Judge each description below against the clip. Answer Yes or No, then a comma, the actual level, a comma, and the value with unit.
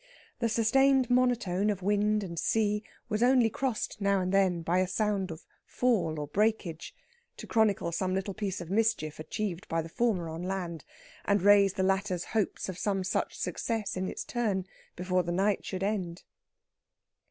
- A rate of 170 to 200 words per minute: Yes, average, 175 wpm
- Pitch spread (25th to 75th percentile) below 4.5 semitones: Yes, average, 3.1 semitones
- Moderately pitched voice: No, high, 195 Hz